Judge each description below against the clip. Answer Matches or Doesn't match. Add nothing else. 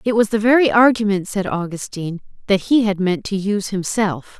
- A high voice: Matches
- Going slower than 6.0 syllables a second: Matches